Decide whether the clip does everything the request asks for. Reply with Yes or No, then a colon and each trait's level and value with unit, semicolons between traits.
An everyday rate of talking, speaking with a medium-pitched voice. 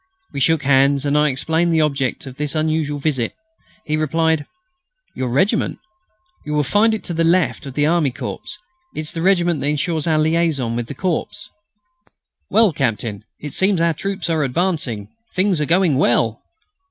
Yes: average, 175 wpm; medium, 155 Hz